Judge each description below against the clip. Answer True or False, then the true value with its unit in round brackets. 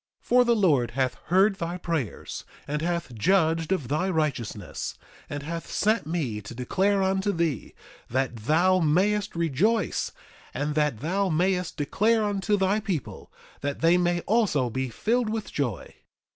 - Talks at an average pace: True (155 wpm)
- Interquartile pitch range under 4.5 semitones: False (5.4 semitones)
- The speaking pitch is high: False (170 Hz)